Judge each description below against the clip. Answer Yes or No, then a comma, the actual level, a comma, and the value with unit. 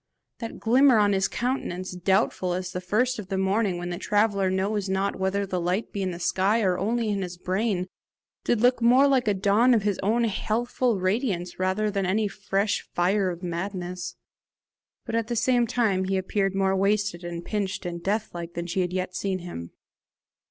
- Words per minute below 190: No, average, 195 wpm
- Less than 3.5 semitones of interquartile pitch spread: Yes, average, 2.9 semitones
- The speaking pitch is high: Yes, high, 195 Hz